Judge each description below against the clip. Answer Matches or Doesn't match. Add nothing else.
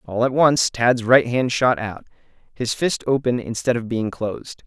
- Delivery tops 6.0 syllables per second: Doesn't match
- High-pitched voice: Doesn't match